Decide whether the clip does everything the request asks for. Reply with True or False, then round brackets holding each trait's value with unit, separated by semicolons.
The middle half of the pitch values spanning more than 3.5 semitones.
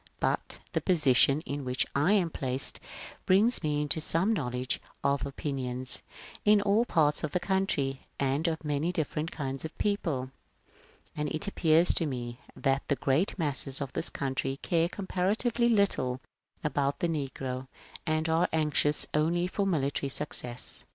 True (4.3 semitones)